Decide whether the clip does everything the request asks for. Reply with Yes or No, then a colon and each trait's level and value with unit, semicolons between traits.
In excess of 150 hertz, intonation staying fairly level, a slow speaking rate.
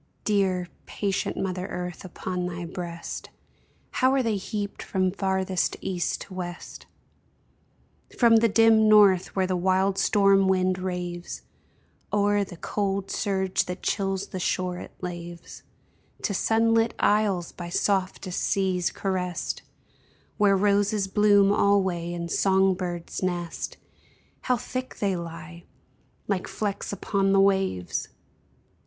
Yes: high, 190 Hz; narrow, 2.1 semitones; slow, 125 wpm